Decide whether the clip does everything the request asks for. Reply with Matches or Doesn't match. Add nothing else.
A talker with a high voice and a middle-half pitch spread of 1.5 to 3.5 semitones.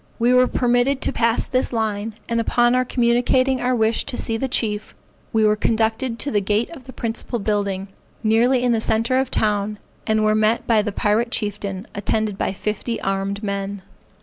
Matches